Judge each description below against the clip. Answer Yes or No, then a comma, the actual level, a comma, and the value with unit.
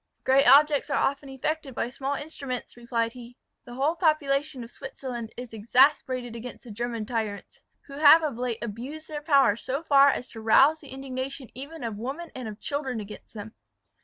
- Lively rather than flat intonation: No, average, 3.4 semitones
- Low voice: No, very high, 260 Hz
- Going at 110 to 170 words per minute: No, average, 185 wpm